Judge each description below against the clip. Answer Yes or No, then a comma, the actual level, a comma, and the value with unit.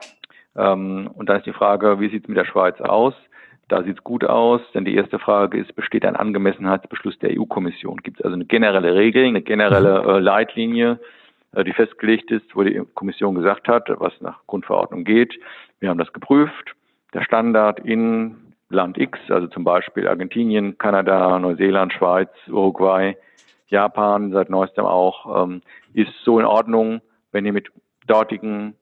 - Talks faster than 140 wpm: Yes, average, 160 wpm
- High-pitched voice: No, low, 105 Hz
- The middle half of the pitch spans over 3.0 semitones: No, narrow, 2.6 semitones